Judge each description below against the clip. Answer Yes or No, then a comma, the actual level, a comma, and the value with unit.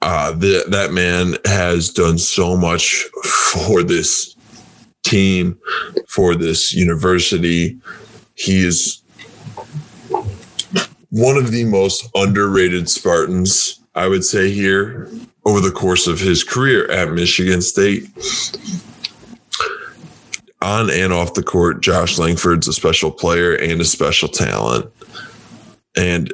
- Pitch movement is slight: Yes, narrow, 2.2 semitones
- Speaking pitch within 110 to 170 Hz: No, very low, 90 Hz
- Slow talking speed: Yes, slow, 115 wpm